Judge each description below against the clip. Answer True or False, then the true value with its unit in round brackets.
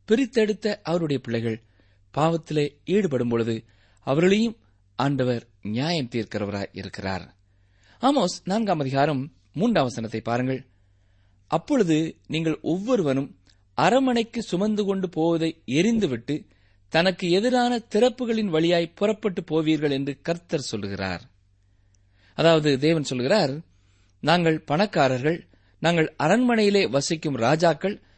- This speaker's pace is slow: False (85 wpm)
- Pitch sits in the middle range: True (150 Hz)